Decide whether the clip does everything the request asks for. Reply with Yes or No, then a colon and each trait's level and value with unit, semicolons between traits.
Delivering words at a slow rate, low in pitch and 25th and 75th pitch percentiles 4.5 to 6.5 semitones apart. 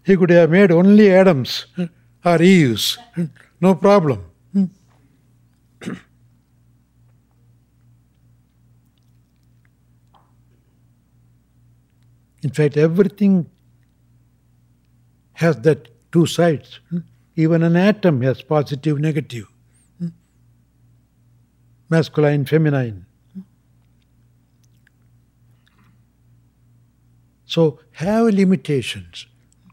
Yes: slow, 55 wpm; low, 120 Hz; average, 5.2 semitones